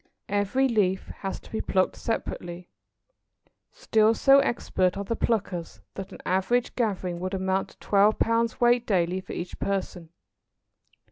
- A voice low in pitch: No, high, 200 Hz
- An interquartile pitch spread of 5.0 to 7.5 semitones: No, average, 3.7 semitones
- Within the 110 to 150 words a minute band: Yes, average, 145 wpm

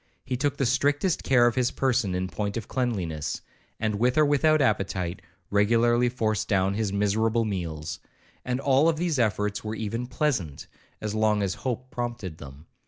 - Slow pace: No, average, 170 wpm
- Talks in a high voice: No, low, 110 Hz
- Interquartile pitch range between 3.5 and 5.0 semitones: Yes, average, 4.1 semitones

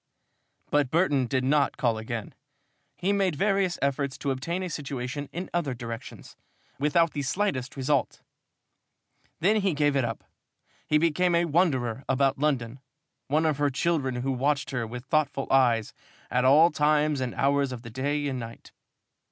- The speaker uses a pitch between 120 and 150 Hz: Yes, medium, 140 Hz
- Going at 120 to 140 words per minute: No, average, 160 wpm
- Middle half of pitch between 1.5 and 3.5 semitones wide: Yes, average, 3.2 semitones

